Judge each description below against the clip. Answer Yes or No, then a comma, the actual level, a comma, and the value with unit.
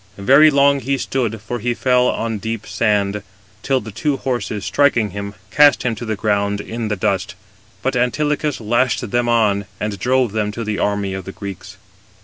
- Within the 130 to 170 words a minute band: No, average, 185 wpm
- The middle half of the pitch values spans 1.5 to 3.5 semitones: No, average, 3.9 semitones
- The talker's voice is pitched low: Yes, low, 115 Hz